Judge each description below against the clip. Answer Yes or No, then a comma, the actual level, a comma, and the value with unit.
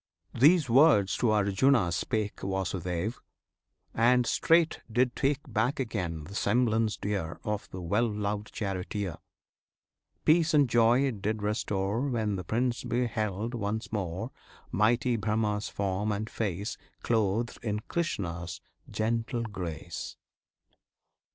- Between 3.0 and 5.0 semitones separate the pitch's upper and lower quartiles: Yes, average, 3.5 semitones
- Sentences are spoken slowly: Yes, slow, 120 wpm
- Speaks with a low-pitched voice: Yes, low, 110 Hz